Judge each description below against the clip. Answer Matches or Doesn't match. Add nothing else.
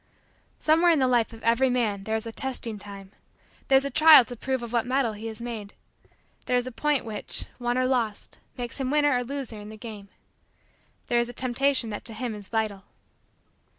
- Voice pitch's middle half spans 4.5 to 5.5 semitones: Doesn't match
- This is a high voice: Matches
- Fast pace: Matches